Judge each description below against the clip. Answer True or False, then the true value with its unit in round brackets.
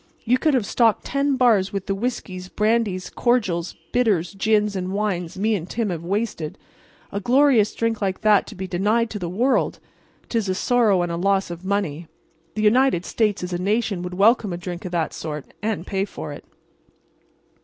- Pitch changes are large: False (3.8 semitones)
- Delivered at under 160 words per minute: False (190 wpm)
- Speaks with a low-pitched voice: False (200 Hz)